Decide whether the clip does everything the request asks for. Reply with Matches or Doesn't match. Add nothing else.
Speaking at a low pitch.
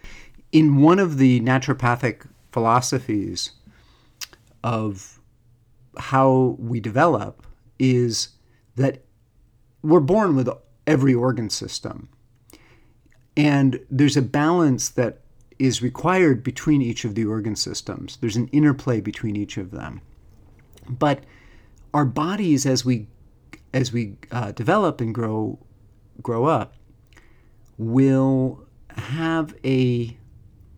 Matches